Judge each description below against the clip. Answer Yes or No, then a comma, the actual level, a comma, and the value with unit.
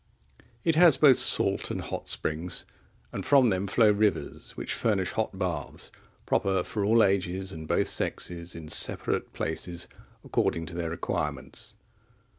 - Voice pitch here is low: Yes, very low, 95 Hz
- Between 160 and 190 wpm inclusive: No, average, 145 wpm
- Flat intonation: No, average, 4.1 semitones